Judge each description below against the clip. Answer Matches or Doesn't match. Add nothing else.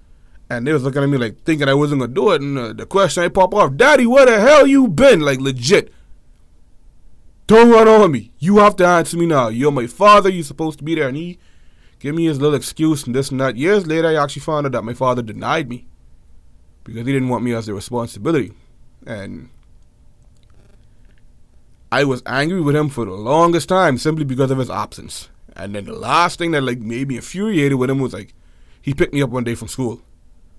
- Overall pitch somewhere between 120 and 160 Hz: Matches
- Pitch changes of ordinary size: Doesn't match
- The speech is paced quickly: Matches